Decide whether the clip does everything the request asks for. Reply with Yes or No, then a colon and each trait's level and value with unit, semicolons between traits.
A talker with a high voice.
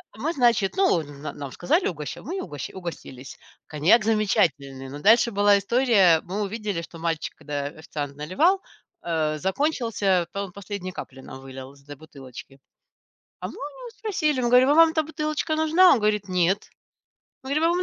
Yes: high, 195 Hz